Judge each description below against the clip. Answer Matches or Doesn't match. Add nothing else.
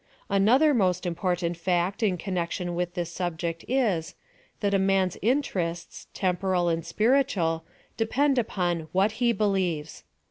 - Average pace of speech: Doesn't match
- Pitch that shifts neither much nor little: Matches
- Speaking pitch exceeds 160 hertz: Matches